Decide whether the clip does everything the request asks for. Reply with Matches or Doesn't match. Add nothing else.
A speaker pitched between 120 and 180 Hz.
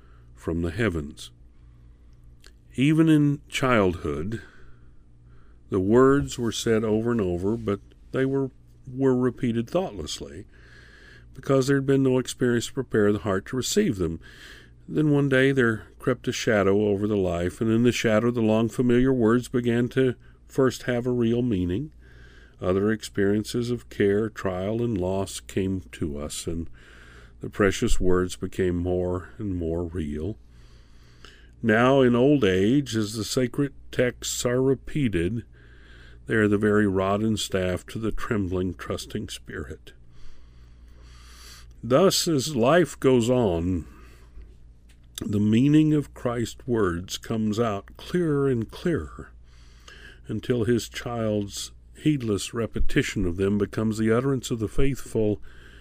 Doesn't match